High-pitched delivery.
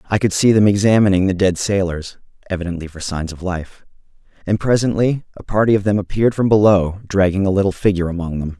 No: very low, 95 Hz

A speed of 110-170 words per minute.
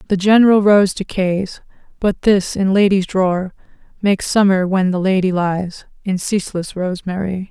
Yes: average, 145 wpm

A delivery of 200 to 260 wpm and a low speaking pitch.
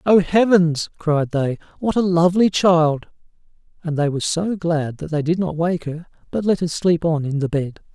No: fast, 205 wpm; medium, 165 Hz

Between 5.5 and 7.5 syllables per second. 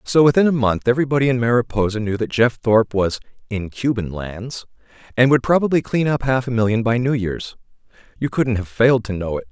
Yes: 5.9 syllables/s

